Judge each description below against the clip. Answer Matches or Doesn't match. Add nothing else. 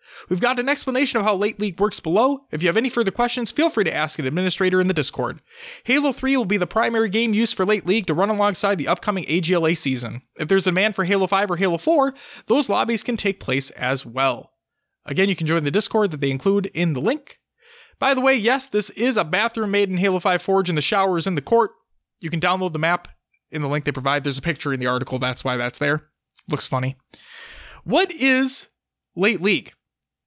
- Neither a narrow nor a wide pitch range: Doesn't match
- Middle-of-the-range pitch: Doesn't match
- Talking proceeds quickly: Matches